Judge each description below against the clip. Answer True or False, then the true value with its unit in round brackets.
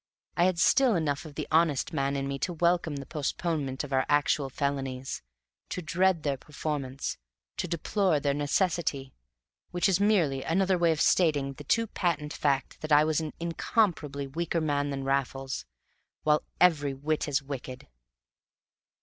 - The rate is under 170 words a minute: True (160 wpm)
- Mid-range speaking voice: True (150 Hz)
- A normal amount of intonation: True (3.7 semitones)